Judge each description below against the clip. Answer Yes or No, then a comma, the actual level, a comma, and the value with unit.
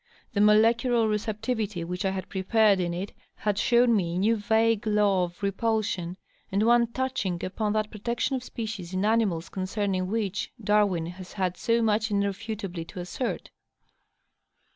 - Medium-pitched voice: No, high, 210 Hz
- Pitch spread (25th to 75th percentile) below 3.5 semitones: Yes, average, 3.1 semitones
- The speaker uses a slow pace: No, average, 155 wpm